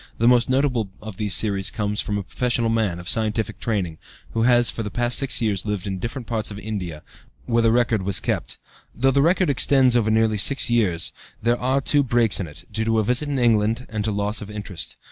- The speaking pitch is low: Yes, low, 110 Hz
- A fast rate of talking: Yes, fast, 225 wpm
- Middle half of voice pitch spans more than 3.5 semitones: No, average, 2.9 semitones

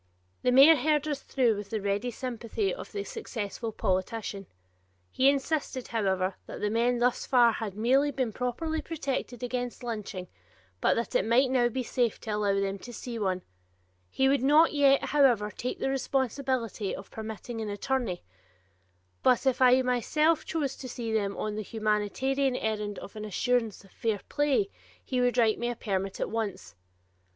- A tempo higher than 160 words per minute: Yes, average, 175 wpm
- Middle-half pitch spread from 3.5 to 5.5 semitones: Yes, average, 4.0 semitones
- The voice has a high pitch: Yes, high, 240 Hz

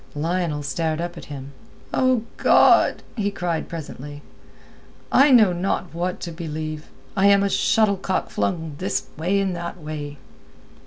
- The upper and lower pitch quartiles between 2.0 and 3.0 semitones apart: No, average, 3.8 semitones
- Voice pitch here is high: No, medium, 170 Hz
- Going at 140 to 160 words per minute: Yes, average, 150 wpm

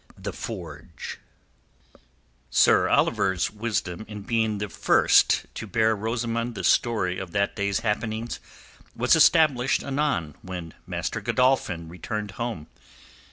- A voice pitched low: Yes, low, 105 Hz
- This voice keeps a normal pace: No, slow, 115 wpm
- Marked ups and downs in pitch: No, average, 3.8 semitones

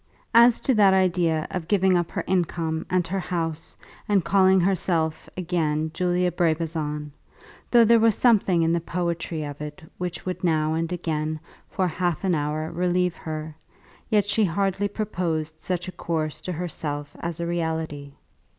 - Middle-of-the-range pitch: Yes, medium, 170 Hz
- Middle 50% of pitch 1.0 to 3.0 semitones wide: Yes, average, 2.7 semitones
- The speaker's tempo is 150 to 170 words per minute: Yes, average, 160 wpm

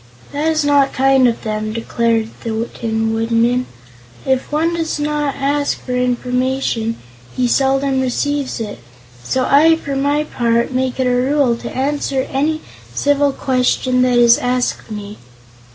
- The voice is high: Yes, very high, 260 Hz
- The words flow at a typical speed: Yes, average, 150 wpm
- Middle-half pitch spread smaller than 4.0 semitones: Yes, average, 3.2 semitones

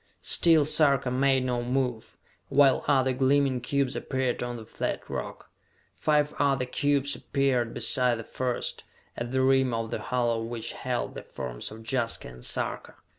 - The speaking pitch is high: No, low, 130 Hz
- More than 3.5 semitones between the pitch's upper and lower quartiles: No, narrow, 2.4 semitones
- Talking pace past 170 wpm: No, average, 160 wpm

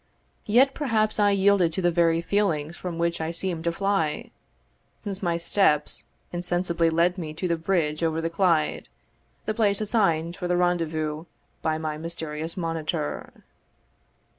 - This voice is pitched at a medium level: Yes, medium, 170 Hz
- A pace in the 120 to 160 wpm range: Yes, average, 150 wpm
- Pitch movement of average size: Yes, average, 3.1 semitones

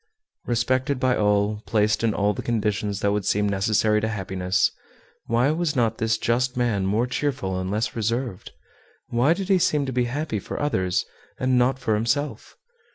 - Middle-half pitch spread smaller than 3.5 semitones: No, average, 3.8 semitones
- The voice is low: Yes, low, 115 Hz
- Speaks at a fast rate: No, average, 175 wpm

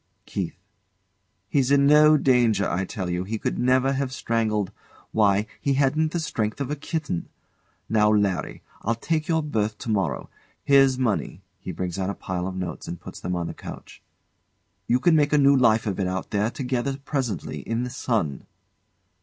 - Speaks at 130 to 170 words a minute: No, average, 185 wpm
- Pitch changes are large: Yes, wide, 5.9 semitones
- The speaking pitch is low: Yes, low, 115 Hz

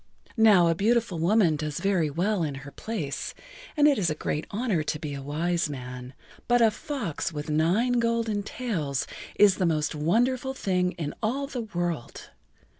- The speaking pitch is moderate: Yes, medium, 180 Hz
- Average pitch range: No, wide, 6.9 semitones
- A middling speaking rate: Yes, average, 175 wpm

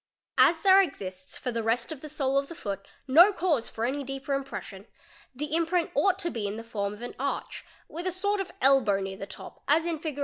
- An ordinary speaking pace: No, fast, 235 wpm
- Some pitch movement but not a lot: No, wide, 6.6 semitones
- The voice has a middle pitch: No, very high, 275 Hz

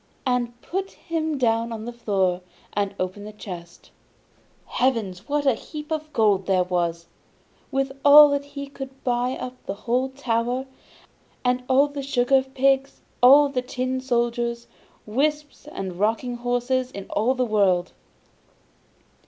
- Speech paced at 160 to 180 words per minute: No, average, 145 wpm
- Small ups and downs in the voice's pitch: No, average, 4.1 semitones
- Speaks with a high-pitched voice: Yes, very high, 250 Hz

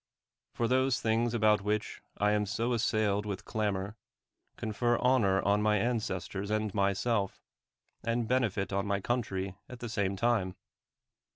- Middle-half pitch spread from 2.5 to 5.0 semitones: Yes, average, 2.9 semitones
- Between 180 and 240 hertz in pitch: No, low, 105 Hz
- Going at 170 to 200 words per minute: No, average, 155 wpm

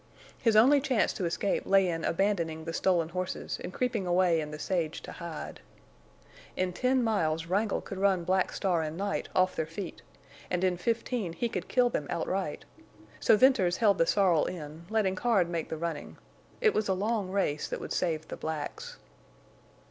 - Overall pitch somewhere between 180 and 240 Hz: Yes, medium, 185 Hz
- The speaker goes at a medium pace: Yes, average, 185 wpm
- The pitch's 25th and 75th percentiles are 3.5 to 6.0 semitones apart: Yes, average, 3.9 semitones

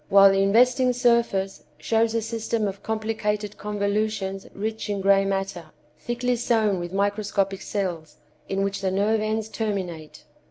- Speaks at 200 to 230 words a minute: No, average, 145 wpm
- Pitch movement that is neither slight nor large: No, narrow, 2.2 semitones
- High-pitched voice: Yes, high, 205 Hz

